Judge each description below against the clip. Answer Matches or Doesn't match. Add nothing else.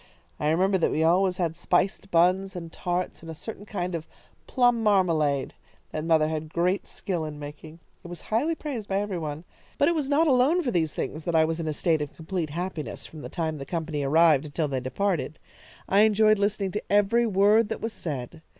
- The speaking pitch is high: Doesn't match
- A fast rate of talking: Matches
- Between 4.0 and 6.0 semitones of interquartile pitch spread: Matches